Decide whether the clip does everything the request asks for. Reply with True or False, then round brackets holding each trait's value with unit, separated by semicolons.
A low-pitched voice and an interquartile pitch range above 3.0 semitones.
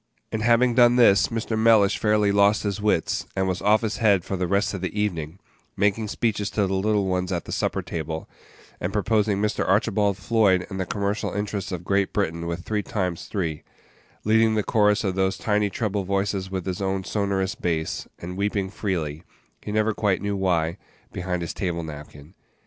False (100 Hz; 2.4 semitones)